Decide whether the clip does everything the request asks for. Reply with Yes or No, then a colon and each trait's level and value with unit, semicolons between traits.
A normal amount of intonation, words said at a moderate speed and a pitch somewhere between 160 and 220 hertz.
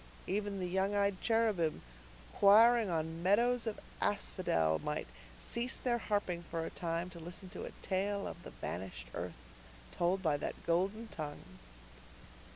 Yes: average, 3.7 semitones; average, 150 wpm; high, 190 Hz